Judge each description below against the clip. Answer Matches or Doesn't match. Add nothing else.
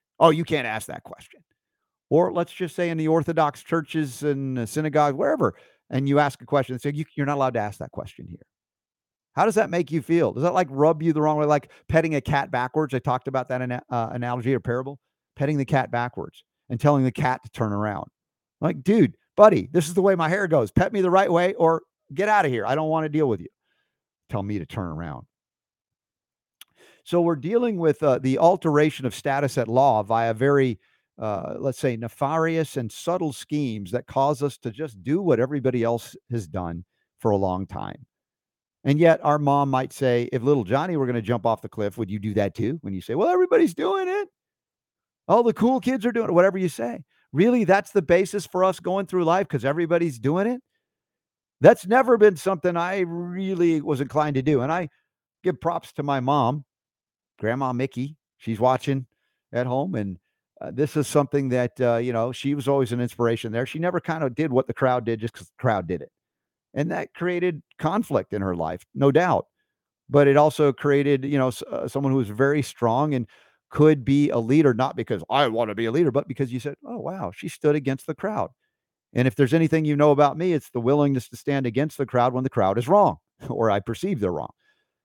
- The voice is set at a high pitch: Doesn't match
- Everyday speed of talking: Doesn't match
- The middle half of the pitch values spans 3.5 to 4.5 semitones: Doesn't match